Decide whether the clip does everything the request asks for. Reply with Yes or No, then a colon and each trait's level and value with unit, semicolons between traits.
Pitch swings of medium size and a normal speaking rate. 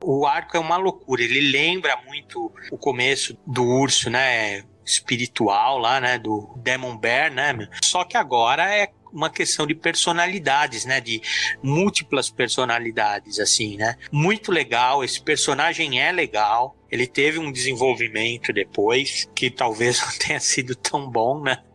No: wide, 6.0 semitones; average, 145 wpm